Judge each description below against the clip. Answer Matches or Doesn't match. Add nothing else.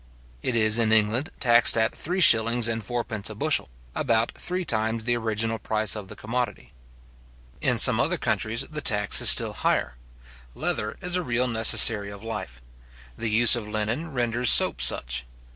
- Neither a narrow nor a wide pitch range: Doesn't match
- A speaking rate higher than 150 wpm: Matches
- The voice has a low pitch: Matches